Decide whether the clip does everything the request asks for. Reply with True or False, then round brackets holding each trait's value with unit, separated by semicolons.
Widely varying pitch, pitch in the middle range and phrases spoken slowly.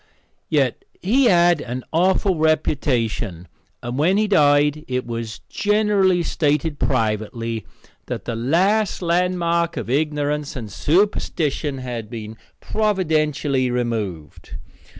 True (6.5 semitones; 150 Hz; 110 wpm)